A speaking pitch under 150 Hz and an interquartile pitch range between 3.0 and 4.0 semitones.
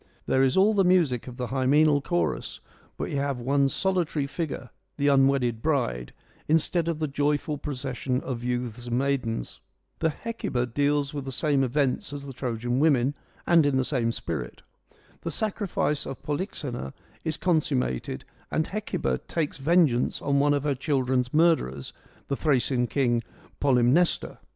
Yes: medium, 140 Hz; average, 3.5 semitones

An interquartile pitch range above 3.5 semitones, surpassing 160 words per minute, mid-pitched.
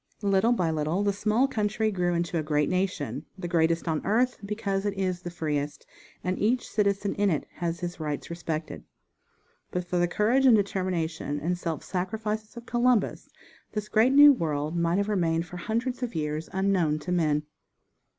Yes: average, 4.3 semitones; average, 180 wpm; medium, 180 Hz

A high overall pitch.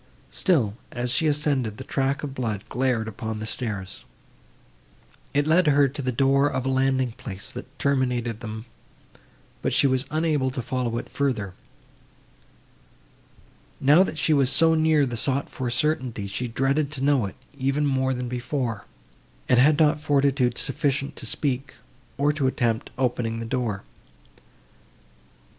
No: low, 130 Hz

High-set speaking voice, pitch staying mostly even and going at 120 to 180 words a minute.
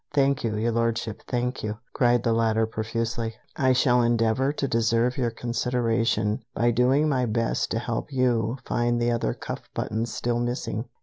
No: low, 120 Hz; narrow, 1.5 semitones; average, 170 wpm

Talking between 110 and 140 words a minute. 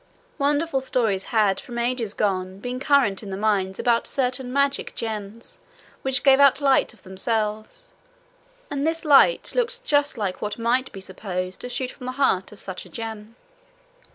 No: average, 170 wpm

